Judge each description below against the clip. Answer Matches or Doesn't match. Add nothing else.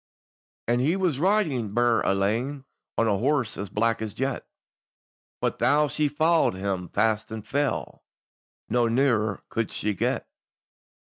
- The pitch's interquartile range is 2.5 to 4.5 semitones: Doesn't match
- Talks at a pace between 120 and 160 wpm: Matches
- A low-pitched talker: Matches